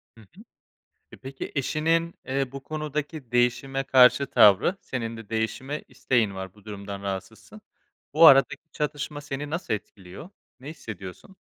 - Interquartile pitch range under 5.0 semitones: No, average, 5.3 semitones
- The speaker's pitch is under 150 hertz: Yes, low, 135 Hz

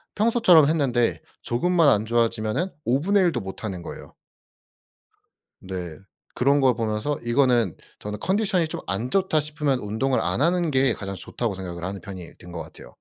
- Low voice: Yes, low, 125 Hz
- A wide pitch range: Yes, wide, 7.3 semitones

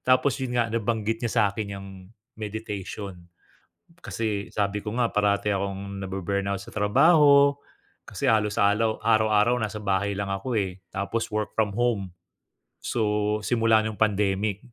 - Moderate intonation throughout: No, narrow, 2.2 semitones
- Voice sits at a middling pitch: No, low, 105 Hz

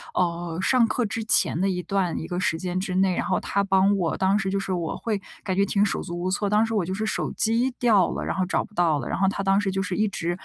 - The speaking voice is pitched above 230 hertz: No, high, 195 Hz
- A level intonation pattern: Yes, narrow, 2.3 semitones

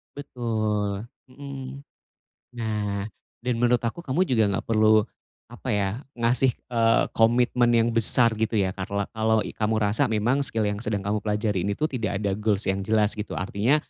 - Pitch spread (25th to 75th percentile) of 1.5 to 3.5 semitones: Yes, average, 2.8 semitones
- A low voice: Yes, low, 110 Hz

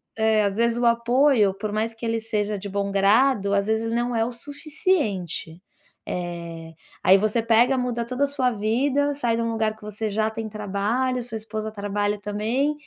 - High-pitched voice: Yes, high, 220 Hz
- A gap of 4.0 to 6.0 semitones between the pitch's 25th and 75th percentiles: No, average, 2.9 semitones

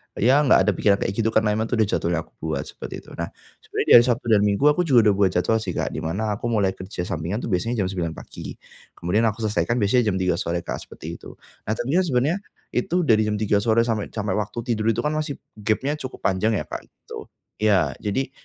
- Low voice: Yes, low, 110 Hz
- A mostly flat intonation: No, average, 3.4 semitones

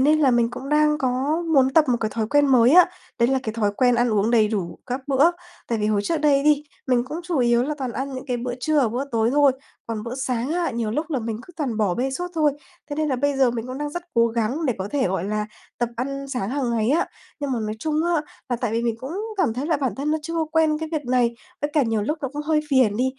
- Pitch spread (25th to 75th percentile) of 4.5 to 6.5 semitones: No, average, 4.1 semitones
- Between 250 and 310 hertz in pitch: Yes, very high, 260 Hz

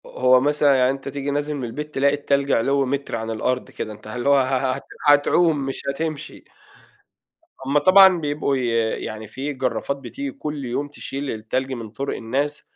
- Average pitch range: No, narrow, 2.3 semitones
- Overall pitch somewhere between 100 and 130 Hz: No, medium, 140 Hz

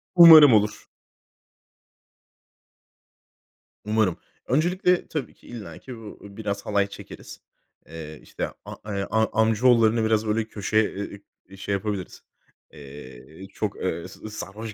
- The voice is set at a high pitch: No, low, 105 Hz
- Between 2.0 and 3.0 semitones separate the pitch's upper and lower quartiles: Yes, narrow, 2.5 semitones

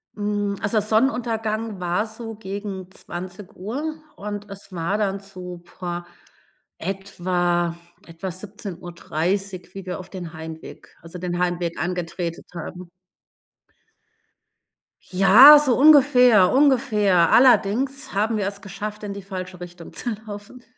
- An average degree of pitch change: Yes, average, 3.2 semitones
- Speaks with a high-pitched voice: Yes, high, 195 Hz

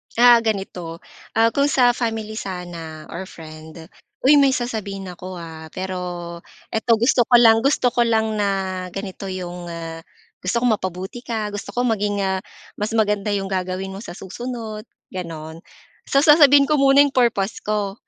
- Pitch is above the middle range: Yes, high, 205 Hz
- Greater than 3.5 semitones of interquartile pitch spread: Yes, average, 4.4 semitones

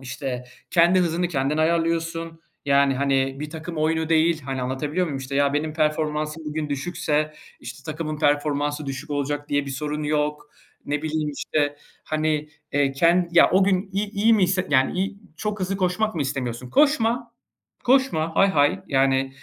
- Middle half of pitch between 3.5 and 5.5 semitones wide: No, average, 3.0 semitones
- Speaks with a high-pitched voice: No, medium, 155 Hz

